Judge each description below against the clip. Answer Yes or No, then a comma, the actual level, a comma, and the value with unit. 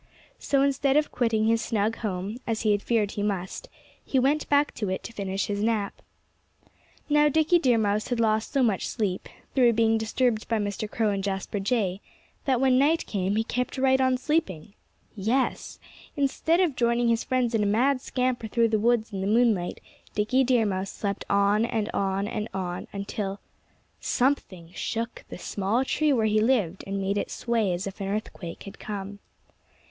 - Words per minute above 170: Yes, average, 185 wpm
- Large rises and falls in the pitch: No, average, 3.9 semitones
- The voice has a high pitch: Yes, high, 220 Hz